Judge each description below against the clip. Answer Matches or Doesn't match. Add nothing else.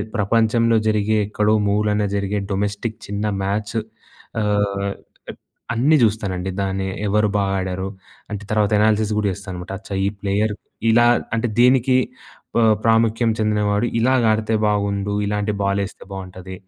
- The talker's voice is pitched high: Doesn't match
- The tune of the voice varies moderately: Doesn't match